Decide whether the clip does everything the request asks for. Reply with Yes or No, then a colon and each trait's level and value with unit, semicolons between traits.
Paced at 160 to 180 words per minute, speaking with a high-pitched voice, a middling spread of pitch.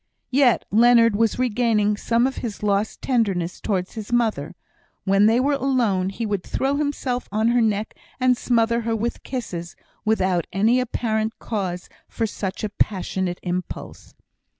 No: average, 150 wpm; high, 220 Hz; average, 3.5 semitones